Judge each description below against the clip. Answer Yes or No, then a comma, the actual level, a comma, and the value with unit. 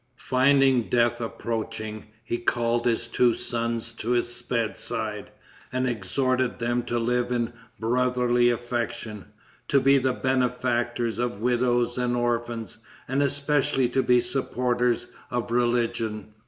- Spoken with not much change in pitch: Yes, narrow, 1.2 semitones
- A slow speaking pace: Yes, slow, 125 wpm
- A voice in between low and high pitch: No, low, 120 Hz